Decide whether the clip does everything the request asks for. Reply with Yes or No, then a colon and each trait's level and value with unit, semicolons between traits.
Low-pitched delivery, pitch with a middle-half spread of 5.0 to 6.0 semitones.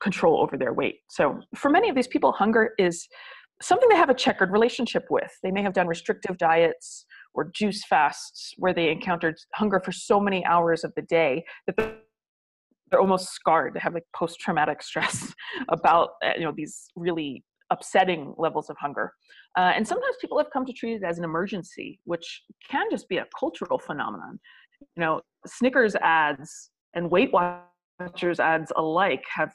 No: medium, 185 Hz; wide, 5.4 semitones